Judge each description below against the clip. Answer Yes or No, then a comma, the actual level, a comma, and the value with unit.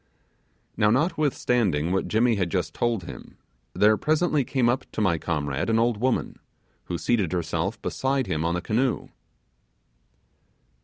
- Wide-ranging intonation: Yes, wide, 6.3 semitones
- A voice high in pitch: No, low, 110 Hz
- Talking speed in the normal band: Yes, average, 145 wpm